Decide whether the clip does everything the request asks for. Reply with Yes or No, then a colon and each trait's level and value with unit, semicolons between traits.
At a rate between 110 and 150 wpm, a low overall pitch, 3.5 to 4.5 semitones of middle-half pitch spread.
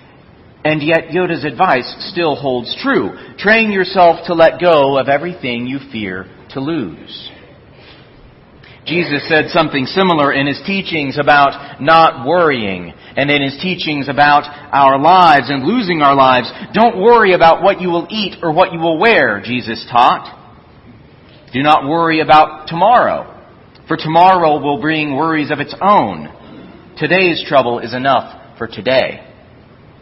No: average, 145 wpm; medium, 155 Hz; average, 4.1 semitones